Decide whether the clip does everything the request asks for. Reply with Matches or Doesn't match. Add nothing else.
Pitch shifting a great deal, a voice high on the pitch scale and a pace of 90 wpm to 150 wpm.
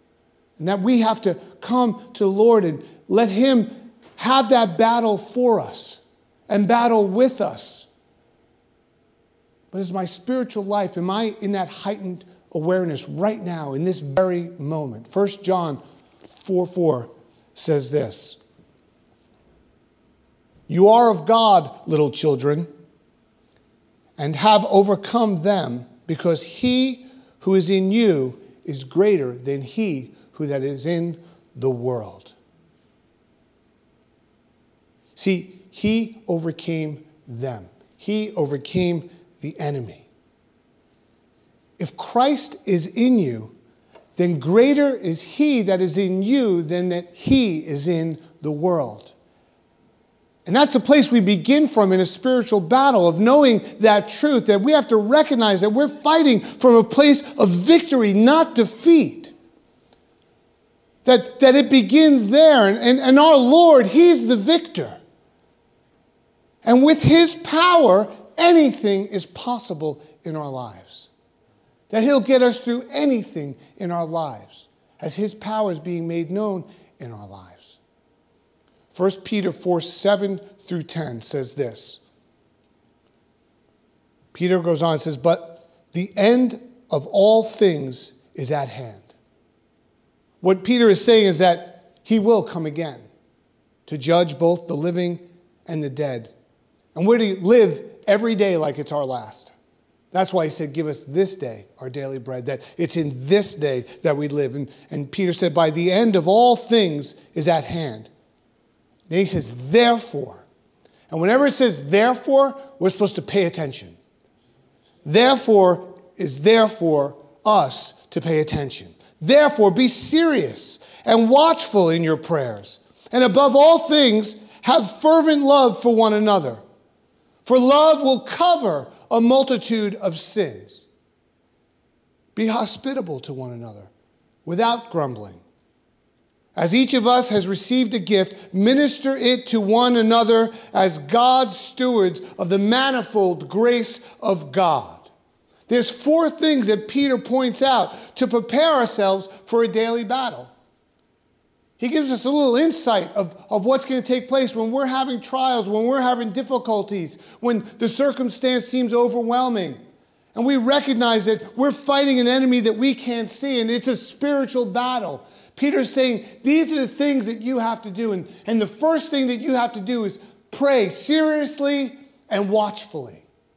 Matches